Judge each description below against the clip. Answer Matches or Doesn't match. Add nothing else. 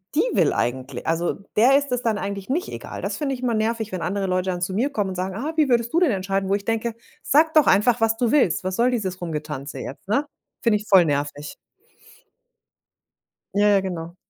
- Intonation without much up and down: Doesn't match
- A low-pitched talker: Doesn't match